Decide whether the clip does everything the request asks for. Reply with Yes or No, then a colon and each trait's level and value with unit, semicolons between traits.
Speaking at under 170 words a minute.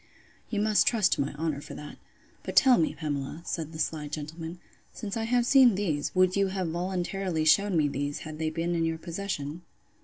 No: fast, 205 wpm